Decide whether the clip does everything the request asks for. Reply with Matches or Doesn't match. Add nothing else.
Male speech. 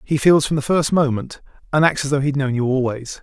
Matches